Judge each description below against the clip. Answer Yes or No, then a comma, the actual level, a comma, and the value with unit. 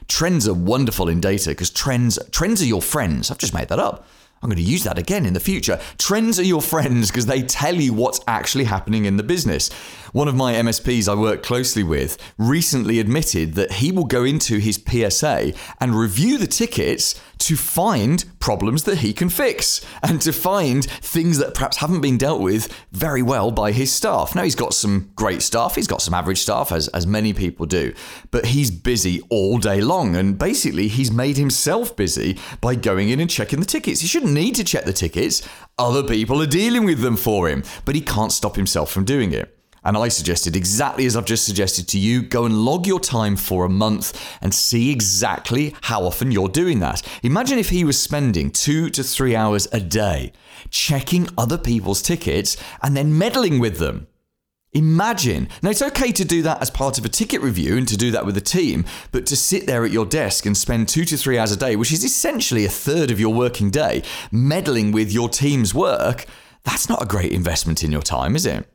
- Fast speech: Yes, fast, 215 wpm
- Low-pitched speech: Yes, low, 120 Hz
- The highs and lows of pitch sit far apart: Yes, wide, 6.1 semitones